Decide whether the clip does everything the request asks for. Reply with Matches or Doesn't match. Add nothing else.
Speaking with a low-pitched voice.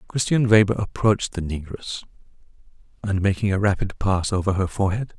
Matches